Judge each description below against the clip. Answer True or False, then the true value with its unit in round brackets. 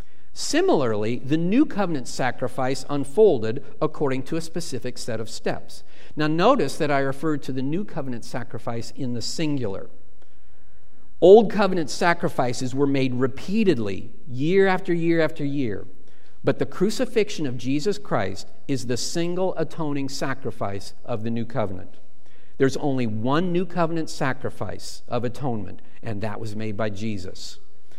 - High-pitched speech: False (135 Hz)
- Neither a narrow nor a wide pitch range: False (6.0 semitones)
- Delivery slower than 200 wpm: True (140 wpm)